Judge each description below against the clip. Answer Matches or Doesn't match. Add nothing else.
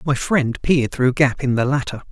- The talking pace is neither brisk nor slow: Doesn't match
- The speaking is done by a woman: Doesn't match